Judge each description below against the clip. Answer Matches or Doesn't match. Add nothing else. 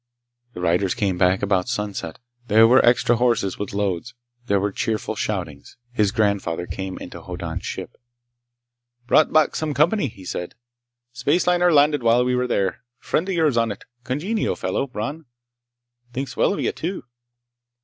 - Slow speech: Doesn't match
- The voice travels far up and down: Matches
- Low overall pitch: Matches